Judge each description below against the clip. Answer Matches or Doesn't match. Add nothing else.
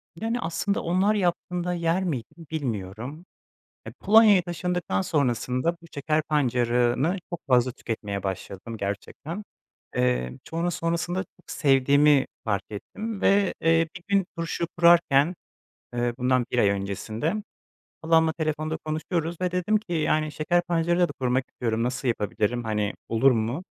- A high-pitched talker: Doesn't match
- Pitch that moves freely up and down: Matches